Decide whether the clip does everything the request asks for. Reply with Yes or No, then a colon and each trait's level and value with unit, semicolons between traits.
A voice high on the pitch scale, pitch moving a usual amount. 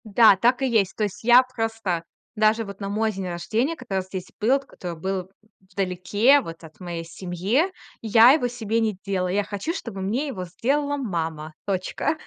Yes: high, 205 Hz; average, 4.6 semitones